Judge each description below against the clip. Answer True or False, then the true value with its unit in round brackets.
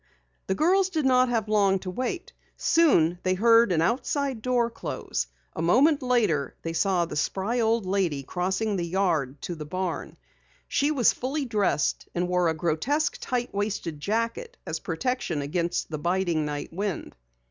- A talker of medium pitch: False (195 Hz)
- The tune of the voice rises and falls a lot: True (6.6 semitones)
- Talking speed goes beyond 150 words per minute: True (165 wpm)